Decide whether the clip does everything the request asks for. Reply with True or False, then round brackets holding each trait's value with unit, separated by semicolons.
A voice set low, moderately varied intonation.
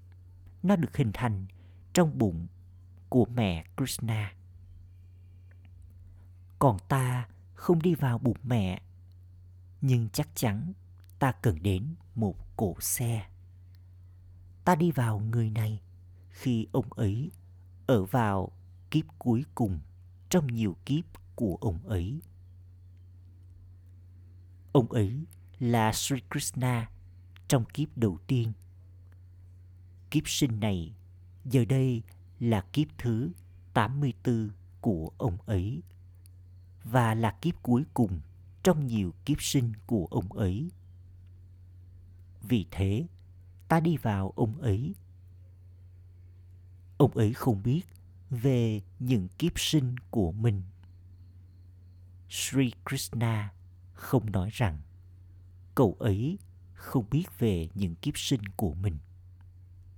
True (95 Hz; 4.7 semitones)